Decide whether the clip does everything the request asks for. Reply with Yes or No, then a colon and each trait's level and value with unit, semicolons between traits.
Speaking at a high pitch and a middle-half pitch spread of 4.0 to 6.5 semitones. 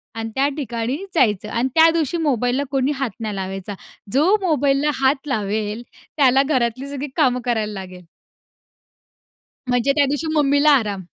Yes: very high, 260 Hz; average, 4.3 semitones